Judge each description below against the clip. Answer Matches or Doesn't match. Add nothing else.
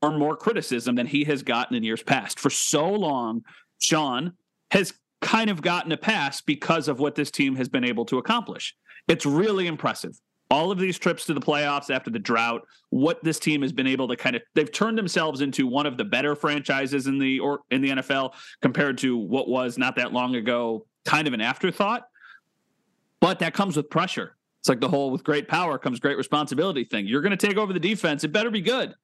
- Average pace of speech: Doesn't match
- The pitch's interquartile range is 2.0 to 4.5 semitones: Doesn't match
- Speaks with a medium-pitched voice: Matches